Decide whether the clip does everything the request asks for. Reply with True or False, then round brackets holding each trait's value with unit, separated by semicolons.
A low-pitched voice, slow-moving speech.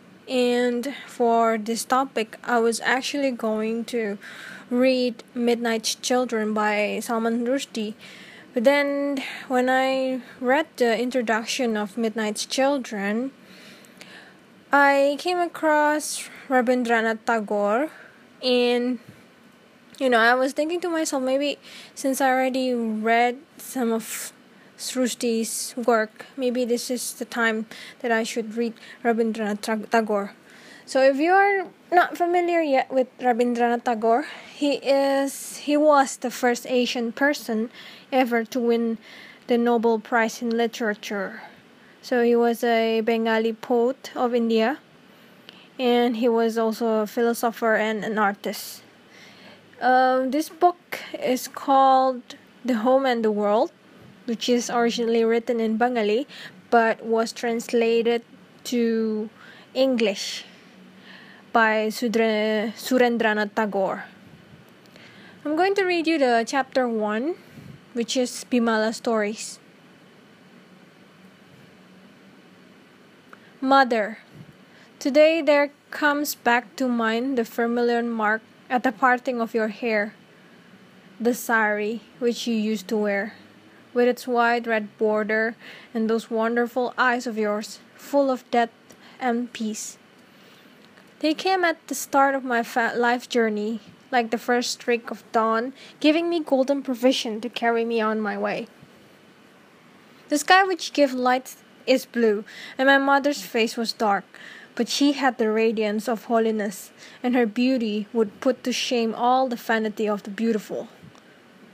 False (235 Hz; 125 wpm)